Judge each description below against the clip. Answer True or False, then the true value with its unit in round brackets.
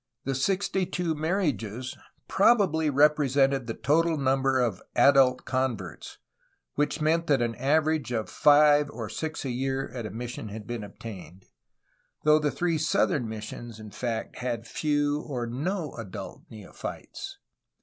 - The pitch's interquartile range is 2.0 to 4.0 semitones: False (4.6 semitones)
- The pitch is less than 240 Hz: True (135 Hz)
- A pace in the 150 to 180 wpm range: False (140 wpm)